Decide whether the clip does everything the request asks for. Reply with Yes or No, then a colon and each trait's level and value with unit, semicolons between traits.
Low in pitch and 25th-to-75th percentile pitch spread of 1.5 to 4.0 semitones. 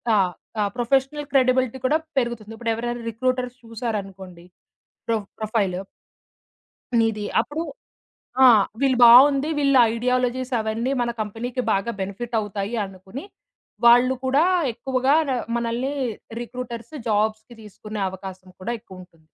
No: high, 235 Hz; average, 3.4 semitones